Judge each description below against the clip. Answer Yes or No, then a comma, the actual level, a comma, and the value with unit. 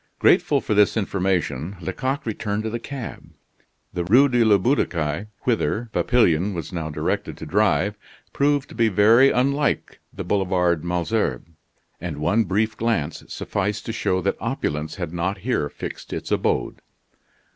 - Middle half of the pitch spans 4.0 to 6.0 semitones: Yes, average, 4.8 semitones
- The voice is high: No, low, 100 Hz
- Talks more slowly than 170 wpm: Yes, average, 155 wpm